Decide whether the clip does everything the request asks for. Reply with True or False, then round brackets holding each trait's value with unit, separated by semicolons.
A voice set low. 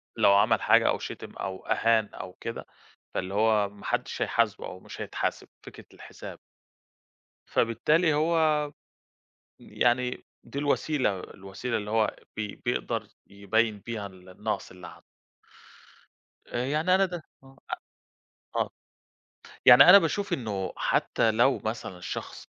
True (115 Hz)